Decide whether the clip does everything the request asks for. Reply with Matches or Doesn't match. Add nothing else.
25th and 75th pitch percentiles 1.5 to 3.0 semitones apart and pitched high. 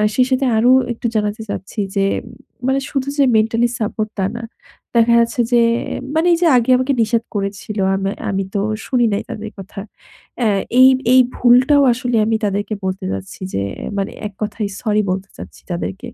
Doesn't match